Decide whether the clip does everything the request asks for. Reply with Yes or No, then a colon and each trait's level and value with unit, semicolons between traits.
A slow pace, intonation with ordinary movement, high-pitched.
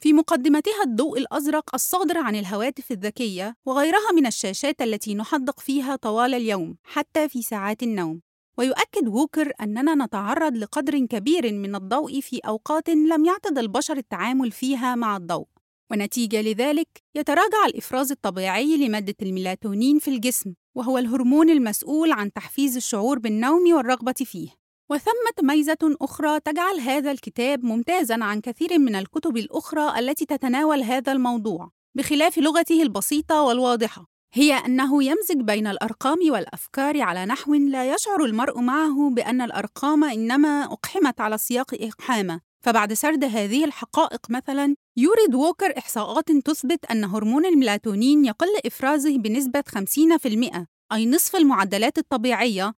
Yes: slow, 130 wpm; average, 5.0 semitones; very high, 265 Hz